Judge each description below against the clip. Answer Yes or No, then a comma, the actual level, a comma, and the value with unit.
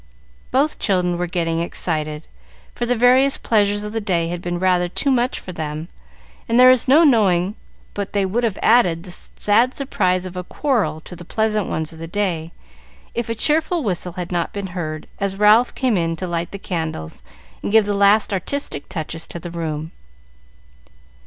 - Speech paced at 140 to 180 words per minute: No, average, 190 wpm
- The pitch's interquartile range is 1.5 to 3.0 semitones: No, average, 4.8 semitones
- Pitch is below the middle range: No, medium, 185 Hz